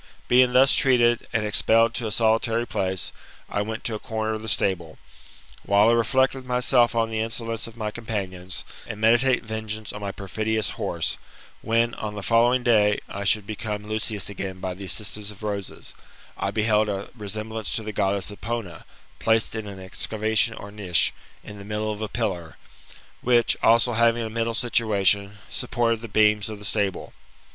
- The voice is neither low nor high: No, low, 110 Hz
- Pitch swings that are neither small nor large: No, narrow, 2.1 semitones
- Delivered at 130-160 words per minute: No, average, 185 wpm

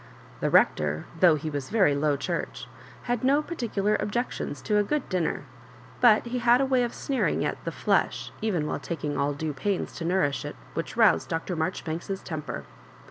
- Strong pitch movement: Yes, wide, 7.8 semitones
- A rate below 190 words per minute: No, average, 200 wpm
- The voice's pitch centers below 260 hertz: Yes, medium, 185 Hz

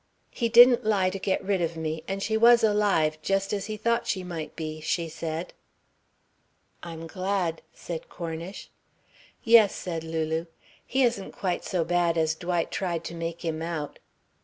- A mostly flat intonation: No, average, 3.7 semitones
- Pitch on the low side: No, medium, 175 Hz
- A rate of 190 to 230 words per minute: No, average, 165 wpm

